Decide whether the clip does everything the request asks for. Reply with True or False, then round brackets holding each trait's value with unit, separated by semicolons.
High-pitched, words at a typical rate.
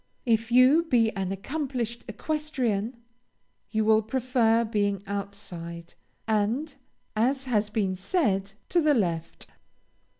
False (220 Hz; 110 wpm)